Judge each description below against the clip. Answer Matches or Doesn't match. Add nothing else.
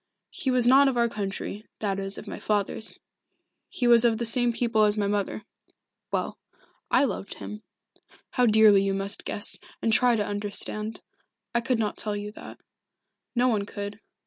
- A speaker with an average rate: Matches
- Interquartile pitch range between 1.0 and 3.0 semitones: Matches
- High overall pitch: Matches